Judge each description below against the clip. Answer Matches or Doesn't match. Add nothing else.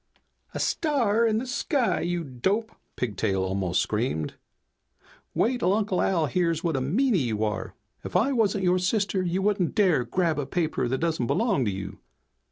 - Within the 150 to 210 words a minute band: Matches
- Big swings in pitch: Matches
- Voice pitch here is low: Doesn't match